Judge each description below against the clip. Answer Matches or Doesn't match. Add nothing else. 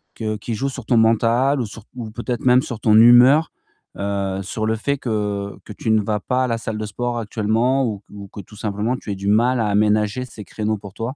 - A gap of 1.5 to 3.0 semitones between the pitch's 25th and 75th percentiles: Matches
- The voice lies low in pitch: Matches